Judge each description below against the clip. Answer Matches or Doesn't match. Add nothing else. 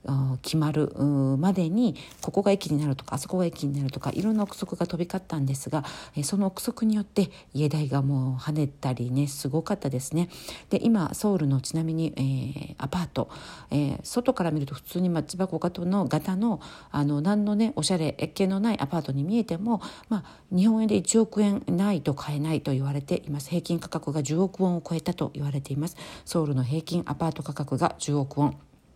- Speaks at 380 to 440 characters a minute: Matches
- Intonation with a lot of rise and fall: Doesn't match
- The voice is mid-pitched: Matches